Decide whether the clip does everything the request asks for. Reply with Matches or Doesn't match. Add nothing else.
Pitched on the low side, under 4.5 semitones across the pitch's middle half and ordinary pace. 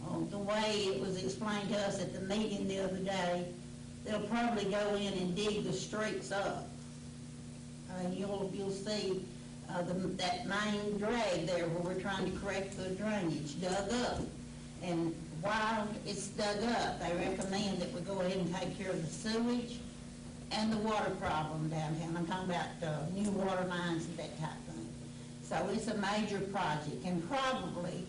Doesn't match